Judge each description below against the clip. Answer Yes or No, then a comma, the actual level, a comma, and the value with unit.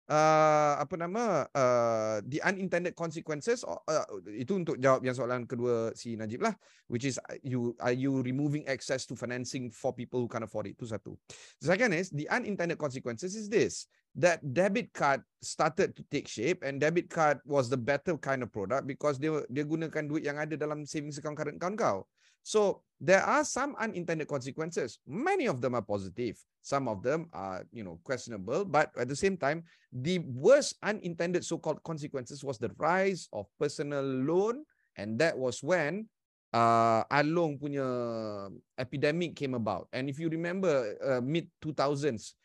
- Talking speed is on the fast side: Yes, fast, 180 wpm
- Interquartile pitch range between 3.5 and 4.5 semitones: No, average, 5.2 semitones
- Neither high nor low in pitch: Yes, medium, 150 Hz